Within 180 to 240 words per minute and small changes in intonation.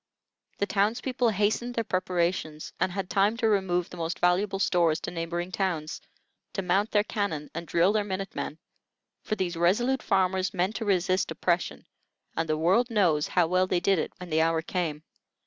No: average, 185 wpm; average, 3.0 semitones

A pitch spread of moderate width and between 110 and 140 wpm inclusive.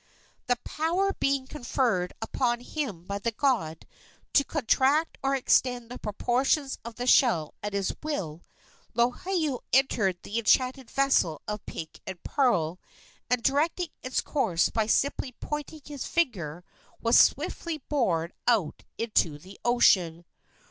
No: wide, 6.1 semitones; slow, 135 wpm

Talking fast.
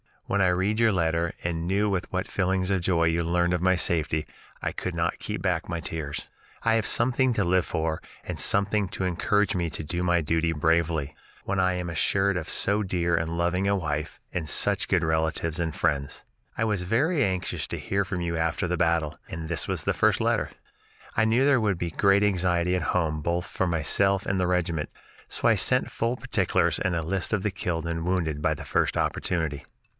Yes: fast, 210 wpm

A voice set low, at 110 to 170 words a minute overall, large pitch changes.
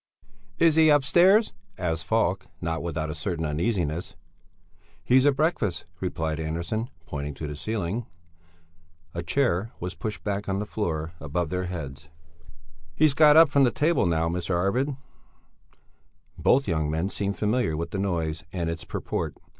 Yes: very low, 90 Hz; average, 155 wpm; wide, 6.9 semitones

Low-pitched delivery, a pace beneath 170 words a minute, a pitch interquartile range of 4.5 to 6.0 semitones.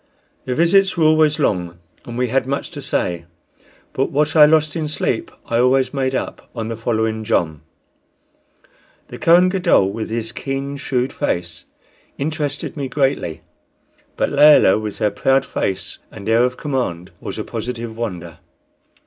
Yes: low, 125 Hz; average, 155 wpm; average, 5.1 semitones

